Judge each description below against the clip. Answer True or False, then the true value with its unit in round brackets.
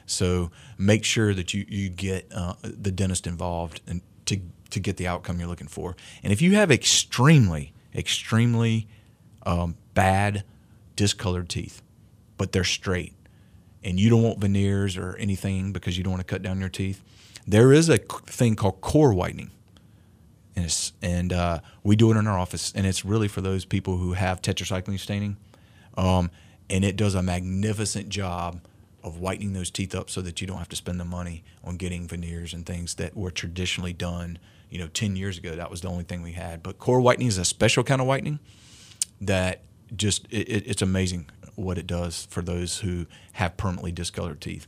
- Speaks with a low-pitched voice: True (95 Hz)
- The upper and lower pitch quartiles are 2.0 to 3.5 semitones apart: True (2.9 semitones)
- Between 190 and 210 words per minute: True (195 wpm)